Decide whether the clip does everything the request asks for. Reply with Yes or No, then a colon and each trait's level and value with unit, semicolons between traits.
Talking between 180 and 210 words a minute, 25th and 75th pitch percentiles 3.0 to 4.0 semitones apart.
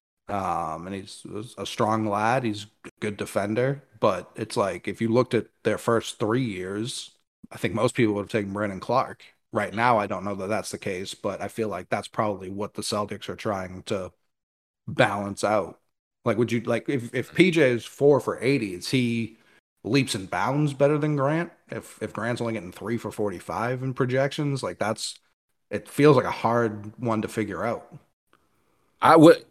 Yes: average, 195 wpm; average, 3.6 semitones